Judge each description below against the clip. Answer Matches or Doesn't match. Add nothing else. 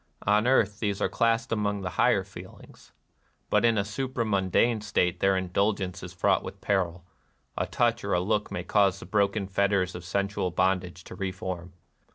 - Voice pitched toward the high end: Doesn't match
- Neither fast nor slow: Matches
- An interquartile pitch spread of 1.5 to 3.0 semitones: Matches